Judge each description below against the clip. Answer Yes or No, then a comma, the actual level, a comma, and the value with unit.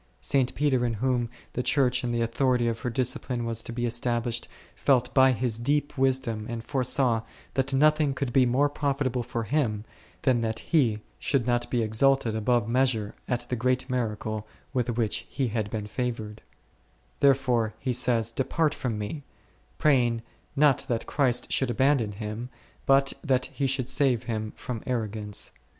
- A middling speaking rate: Yes, average, 165 wpm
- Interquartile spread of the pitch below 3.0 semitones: Yes, narrow, 2.6 semitones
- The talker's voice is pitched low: Yes, low, 125 Hz